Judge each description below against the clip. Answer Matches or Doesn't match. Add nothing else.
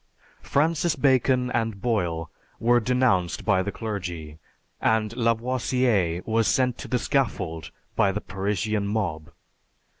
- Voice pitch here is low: Matches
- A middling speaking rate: Doesn't match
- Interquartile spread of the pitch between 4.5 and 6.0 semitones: Matches